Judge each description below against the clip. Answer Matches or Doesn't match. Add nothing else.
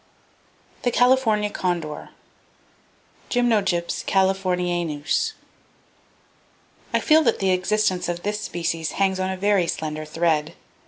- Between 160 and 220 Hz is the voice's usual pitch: Matches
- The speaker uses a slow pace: Matches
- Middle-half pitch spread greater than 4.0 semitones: Doesn't match